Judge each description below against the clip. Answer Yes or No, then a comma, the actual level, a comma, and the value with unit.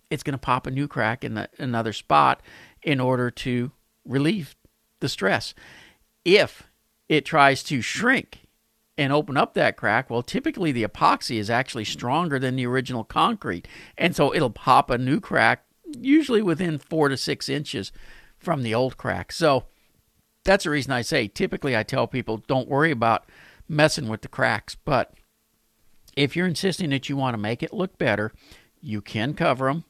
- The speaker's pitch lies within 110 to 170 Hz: Yes, low, 135 Hz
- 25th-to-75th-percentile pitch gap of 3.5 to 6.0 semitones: Yes, average, 4.7 semitones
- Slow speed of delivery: No, average, 175 wpm